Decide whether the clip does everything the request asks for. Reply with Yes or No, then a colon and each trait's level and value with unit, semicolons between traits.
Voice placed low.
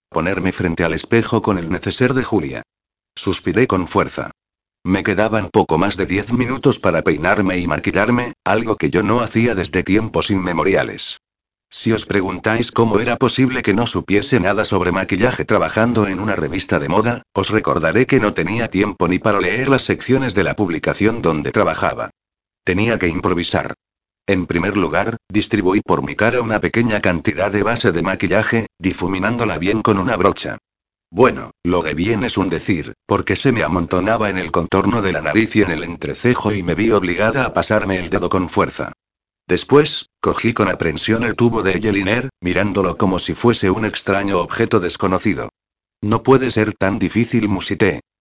Yes: low, 105 Hz